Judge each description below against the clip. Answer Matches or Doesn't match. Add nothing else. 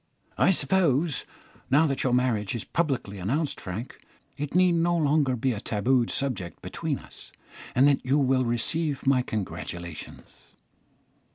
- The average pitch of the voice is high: Doesn't match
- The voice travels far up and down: Doesn't match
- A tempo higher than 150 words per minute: Doesn't match